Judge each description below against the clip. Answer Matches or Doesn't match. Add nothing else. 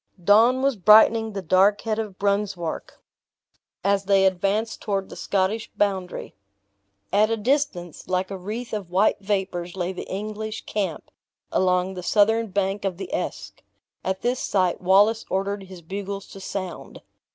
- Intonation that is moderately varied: Doesn't match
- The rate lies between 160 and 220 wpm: Doesn't match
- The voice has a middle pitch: Doesn't match